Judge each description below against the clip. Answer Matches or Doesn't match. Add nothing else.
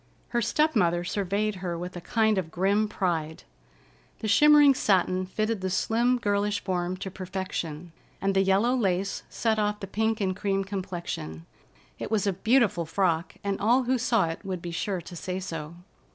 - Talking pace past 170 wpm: Matches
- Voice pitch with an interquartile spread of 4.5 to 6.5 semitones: Doesn't match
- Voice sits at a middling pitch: Doesn't match